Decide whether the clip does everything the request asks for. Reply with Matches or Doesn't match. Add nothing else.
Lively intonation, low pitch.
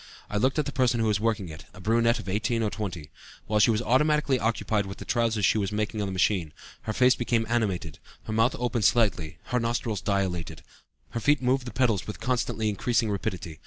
Doesn't match